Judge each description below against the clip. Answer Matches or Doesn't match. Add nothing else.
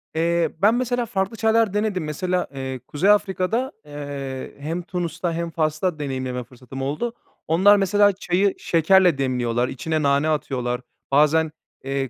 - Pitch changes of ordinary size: Doesn't match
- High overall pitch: Doesn't match